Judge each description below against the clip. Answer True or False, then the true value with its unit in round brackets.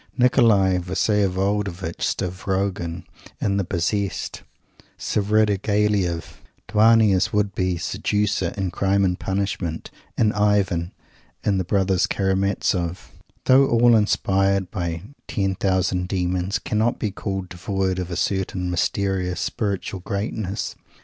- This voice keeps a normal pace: False (110 wpm)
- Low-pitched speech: True (95 Hz)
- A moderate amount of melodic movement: False (2.1 semitones)